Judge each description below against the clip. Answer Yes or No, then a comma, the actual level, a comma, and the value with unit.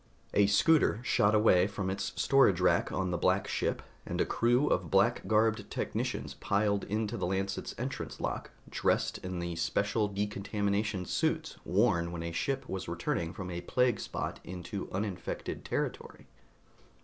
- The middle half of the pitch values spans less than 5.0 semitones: Yes, average, 3.0 semitones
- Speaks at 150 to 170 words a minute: Yes, average, 155 wpm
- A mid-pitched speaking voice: No, low, 100 Hz